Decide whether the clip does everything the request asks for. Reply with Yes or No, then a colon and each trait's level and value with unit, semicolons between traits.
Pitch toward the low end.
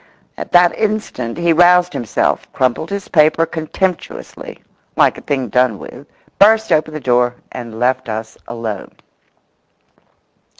No: medium, 155 Hz